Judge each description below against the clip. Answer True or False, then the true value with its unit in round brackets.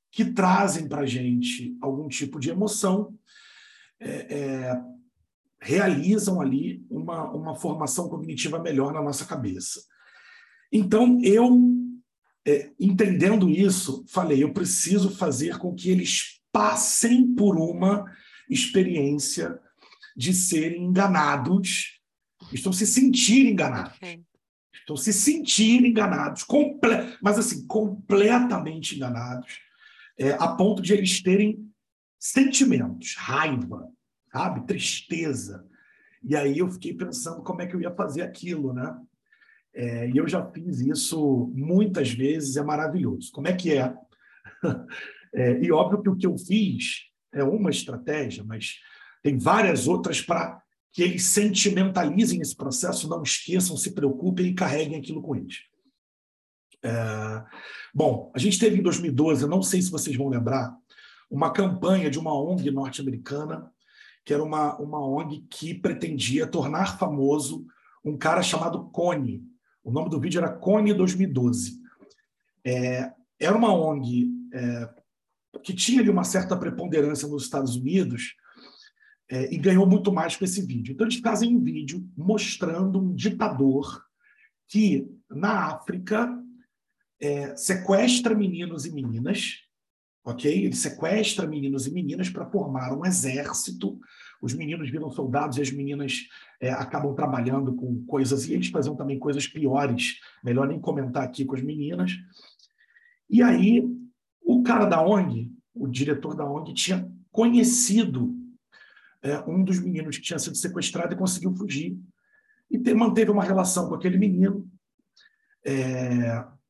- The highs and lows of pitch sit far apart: True (6.7 semitones)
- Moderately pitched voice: True (175 Hz)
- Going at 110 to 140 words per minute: True (135 wpm)